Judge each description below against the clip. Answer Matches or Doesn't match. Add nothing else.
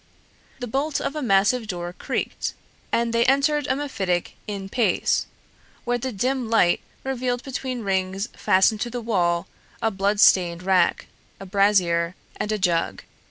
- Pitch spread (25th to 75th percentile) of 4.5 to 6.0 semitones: Matches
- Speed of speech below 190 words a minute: Matches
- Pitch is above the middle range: Matches